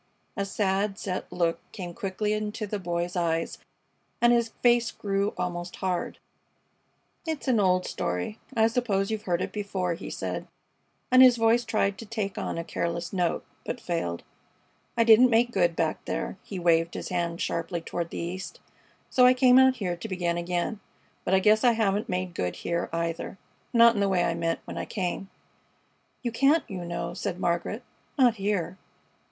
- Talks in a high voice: Yes, high, 195 Hz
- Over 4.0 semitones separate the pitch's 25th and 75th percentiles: Yes, average, 4.5 semitones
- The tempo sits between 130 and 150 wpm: No, average, 180 wpm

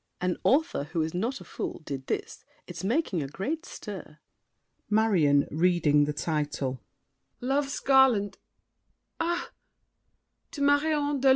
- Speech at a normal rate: No, slow, 125 wpm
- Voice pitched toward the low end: No, high, 205 Hz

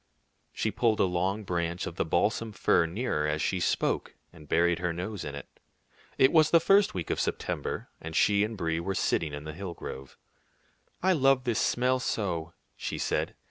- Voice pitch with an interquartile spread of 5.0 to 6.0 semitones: Yes, wide, 5.4 semitones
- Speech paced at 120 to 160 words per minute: No, average, 190 wpm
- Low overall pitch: Yes, very low, 90 Hz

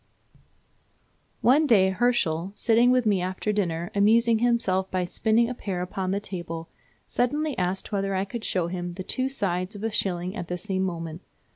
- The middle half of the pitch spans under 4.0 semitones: No, average, 4.3 semitones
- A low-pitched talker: No, high, 195 Hz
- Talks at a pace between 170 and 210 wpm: Yes, average, 175 wpm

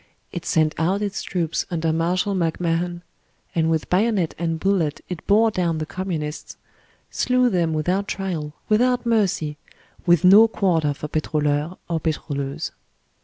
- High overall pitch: No, medium, 170 Hz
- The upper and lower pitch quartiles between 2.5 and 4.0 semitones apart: Yes, average, 3.6 semitones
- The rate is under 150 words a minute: Yes, average, 140 wpm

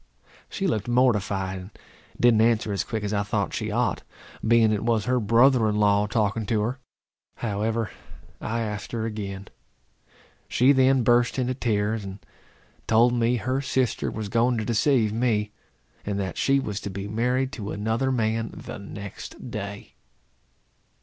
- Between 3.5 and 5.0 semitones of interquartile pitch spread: No, average, 2.8 semitones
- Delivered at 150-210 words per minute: Yes, average, 160 wpm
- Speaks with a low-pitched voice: Yes, low, 110 Hz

